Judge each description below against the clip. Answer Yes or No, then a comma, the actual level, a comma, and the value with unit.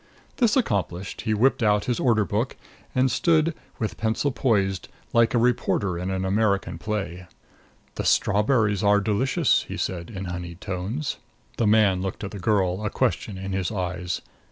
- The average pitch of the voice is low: Yes, low, 105 Hz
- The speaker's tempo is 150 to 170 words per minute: Yes, average, 165 wpm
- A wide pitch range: No, average, 3.4 semitones